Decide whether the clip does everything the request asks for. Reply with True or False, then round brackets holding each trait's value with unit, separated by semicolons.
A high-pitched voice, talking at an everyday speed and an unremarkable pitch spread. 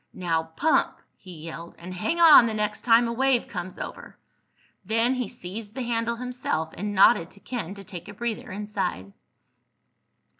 True (210 Hz; 165 wpm; 4.8 semitones)